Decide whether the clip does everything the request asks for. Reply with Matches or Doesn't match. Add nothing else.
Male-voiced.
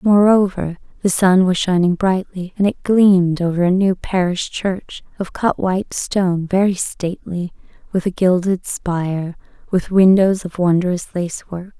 Doesn't match